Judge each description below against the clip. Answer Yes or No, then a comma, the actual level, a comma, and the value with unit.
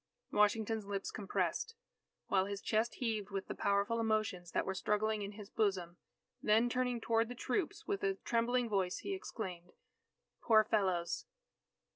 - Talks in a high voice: Yes, high, 215 Hz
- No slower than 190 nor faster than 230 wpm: No, average, 150 wpm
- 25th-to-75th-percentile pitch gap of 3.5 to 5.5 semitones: No, average, 2.8 semitones